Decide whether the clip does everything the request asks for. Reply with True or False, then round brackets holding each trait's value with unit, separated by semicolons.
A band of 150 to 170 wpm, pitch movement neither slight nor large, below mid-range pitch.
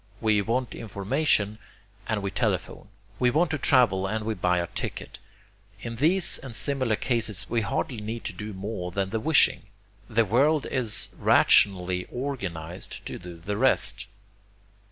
True (155 wpm; 4.6 semitones; 110 Hz)